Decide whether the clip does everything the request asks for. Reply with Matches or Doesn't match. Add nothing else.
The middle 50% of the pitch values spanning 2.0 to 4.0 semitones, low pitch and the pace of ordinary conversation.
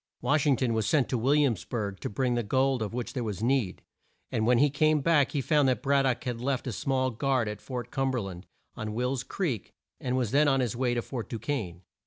Doesn't match